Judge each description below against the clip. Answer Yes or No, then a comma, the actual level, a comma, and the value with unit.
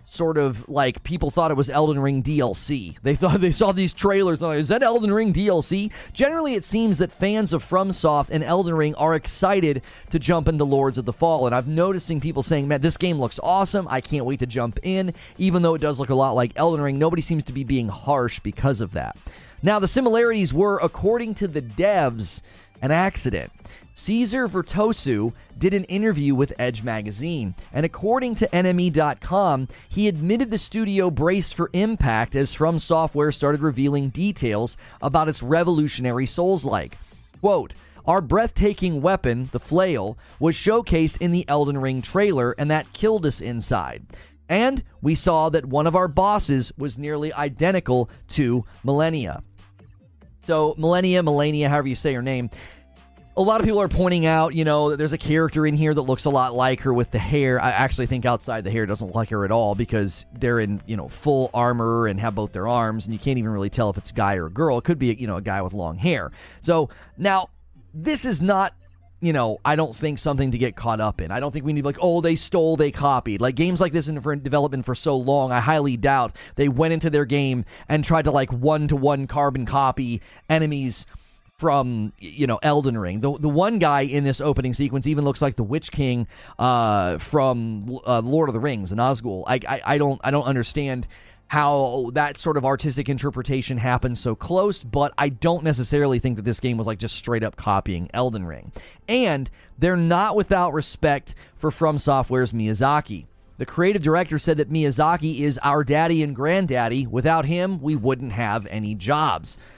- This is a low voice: No, medium, 145 Hz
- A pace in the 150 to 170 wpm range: No, average, 200 wpm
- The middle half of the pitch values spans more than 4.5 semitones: Yes, average, 5.2 semitones